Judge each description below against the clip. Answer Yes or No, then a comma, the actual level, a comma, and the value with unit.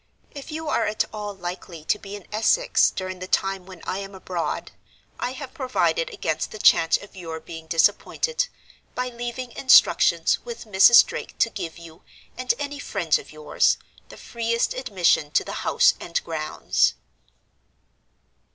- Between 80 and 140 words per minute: No, average, 160 wpm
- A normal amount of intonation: No, wide, 6.1 semitones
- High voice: Yes, high, 210 Hz